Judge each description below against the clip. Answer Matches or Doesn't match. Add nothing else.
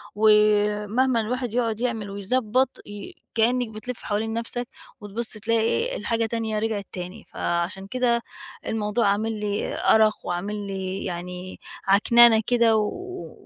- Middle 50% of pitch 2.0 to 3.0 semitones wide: Matches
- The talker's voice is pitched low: Doesn't match